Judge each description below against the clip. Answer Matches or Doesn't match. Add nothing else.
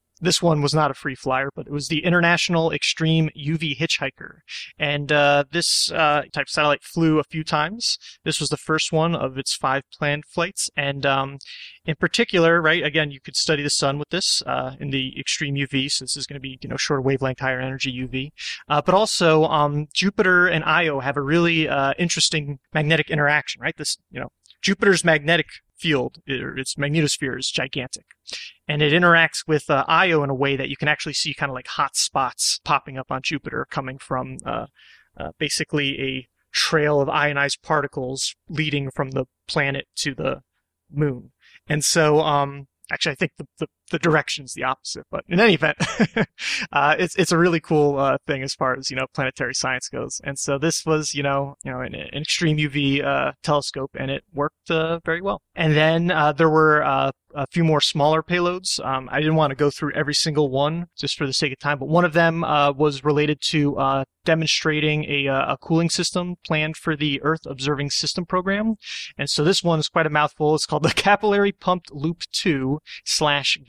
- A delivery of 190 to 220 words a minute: Matches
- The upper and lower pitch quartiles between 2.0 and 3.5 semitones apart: Matches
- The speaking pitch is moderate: Matches